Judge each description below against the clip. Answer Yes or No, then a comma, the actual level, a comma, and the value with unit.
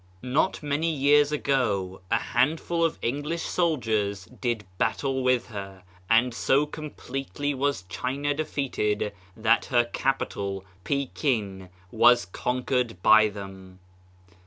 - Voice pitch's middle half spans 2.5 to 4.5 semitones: No, wide, 5.6 semitones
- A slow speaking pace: Yes, slow, 115 wpm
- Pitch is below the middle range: Yes, low, 125 Hz